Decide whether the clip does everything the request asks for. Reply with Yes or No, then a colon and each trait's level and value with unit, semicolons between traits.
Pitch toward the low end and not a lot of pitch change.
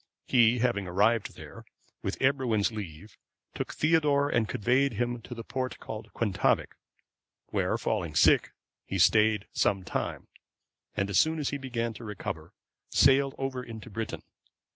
No: low, 115 Hz; average, 3.7 semitones